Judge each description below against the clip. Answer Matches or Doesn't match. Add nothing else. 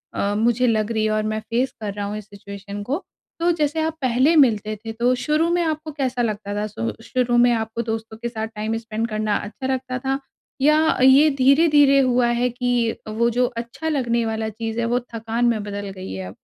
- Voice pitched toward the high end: Matches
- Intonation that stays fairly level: Doesn't match